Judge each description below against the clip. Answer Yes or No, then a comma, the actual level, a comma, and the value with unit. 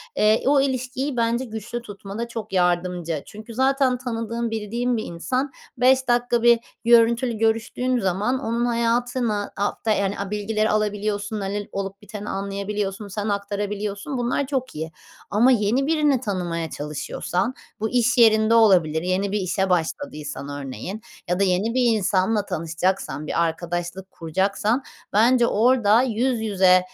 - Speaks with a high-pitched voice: Yes, high, 215 Hz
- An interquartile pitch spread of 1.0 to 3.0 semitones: No, average, 3.7 semitones